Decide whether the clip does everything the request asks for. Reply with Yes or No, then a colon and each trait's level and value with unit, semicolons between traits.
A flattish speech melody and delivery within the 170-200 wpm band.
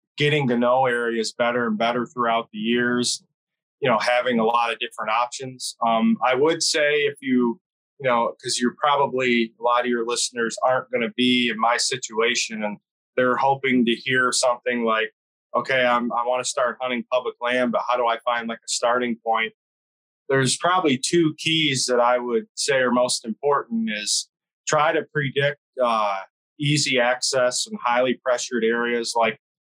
Yes: narrow, 2.1 semitones; average, 180 wpm